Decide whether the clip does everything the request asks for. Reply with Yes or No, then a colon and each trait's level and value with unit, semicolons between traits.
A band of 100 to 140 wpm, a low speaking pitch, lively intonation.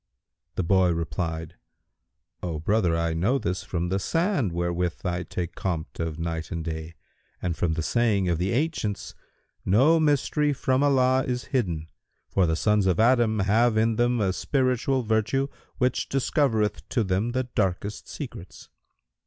No: average, 155 wpm; low, 100 Hz; wide, 6.5 semitones